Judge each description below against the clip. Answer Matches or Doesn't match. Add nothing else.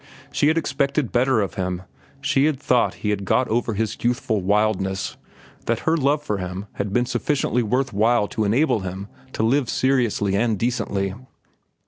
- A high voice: Doesn't match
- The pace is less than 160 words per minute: Doesn't match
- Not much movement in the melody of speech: Doesn't match